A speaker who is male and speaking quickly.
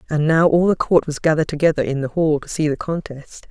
No: female; fast, 255 wpm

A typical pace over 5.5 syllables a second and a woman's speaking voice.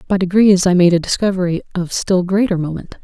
Yes: 5.9 syllables/s; female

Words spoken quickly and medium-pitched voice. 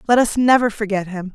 No: fast, 220 wpm; high, 215 Hz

